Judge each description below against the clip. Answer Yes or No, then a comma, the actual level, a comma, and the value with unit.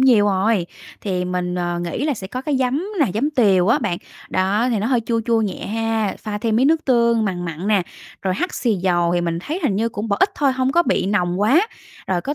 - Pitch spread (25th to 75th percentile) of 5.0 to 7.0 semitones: Yes, average, 5.3 semitones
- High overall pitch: Yes, high, 215 Hz